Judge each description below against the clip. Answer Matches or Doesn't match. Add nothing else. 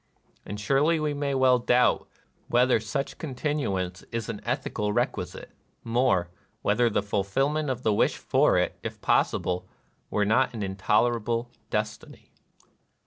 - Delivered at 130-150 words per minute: Matches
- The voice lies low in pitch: Matches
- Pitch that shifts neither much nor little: Matches